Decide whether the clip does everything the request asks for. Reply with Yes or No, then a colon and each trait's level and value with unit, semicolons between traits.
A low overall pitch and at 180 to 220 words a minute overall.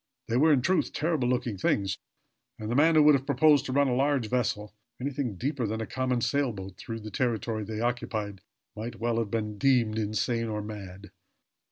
Yes: low, 115 Hz; average, 195 wpm